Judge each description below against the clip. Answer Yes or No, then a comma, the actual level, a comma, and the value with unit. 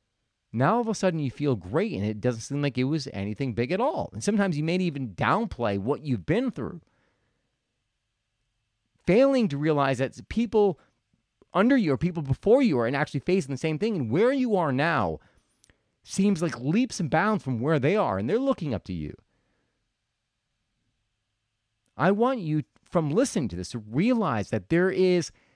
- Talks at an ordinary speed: Yes, average, 185 wpm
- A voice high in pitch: No, medium, 140 Hz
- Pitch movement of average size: No, wide, 8.3 semitones